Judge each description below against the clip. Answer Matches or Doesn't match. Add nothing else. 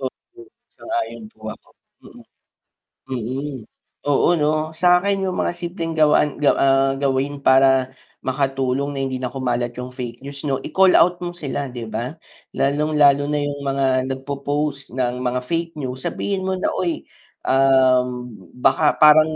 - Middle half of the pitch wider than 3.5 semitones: Doesn't match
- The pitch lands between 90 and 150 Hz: Matches